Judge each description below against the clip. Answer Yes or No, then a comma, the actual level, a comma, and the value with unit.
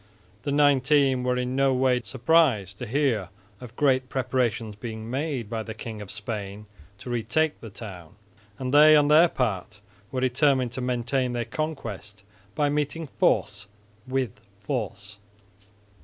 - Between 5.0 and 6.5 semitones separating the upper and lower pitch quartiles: No, average, 4.1 semitones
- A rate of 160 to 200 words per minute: No, average, 145 wpm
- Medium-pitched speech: No, low, 125 Hz